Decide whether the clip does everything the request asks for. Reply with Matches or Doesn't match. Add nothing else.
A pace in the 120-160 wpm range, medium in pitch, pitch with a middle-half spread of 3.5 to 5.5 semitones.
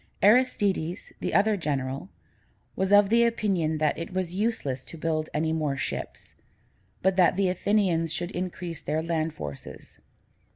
Matches